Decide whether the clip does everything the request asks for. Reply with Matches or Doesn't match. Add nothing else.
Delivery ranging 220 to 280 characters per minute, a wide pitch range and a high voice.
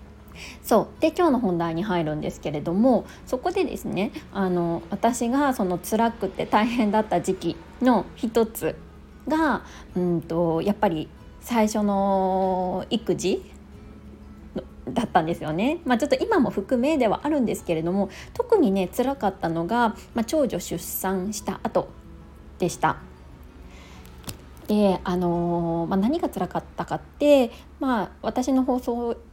Matches